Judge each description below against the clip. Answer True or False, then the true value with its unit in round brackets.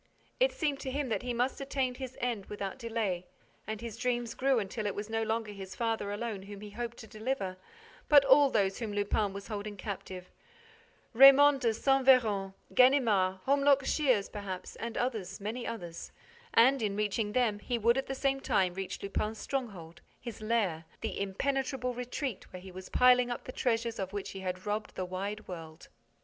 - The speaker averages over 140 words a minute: True (190 wpm)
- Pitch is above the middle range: True (225 Hz)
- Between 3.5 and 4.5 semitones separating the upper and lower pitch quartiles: True (4.2 semitones)